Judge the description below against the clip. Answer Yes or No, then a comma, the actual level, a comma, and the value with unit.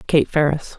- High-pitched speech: No, medium, 140 Hz